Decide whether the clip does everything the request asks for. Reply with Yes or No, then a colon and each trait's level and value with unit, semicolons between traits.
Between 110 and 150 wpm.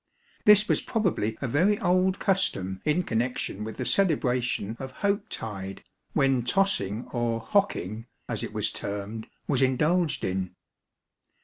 Yes: average, 145 wpm